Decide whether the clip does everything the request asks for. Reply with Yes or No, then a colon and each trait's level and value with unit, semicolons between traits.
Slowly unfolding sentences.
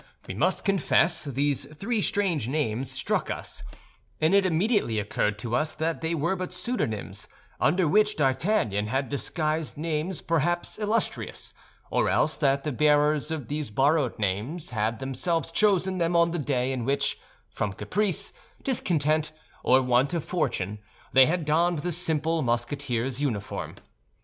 No: average, 150 wpm